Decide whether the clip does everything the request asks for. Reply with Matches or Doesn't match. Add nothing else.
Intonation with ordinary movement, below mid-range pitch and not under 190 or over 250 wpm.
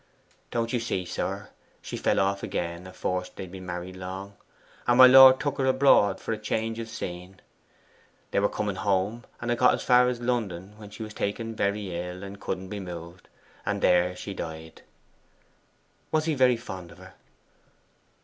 Doesn't match